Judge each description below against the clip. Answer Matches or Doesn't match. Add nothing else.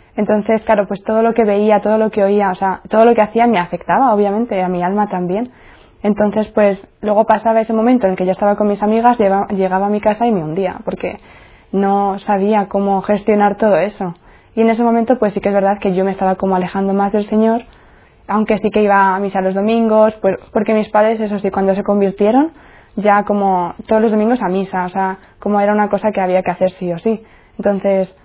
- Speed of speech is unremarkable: Doesn't match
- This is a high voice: Matches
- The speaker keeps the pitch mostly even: Matches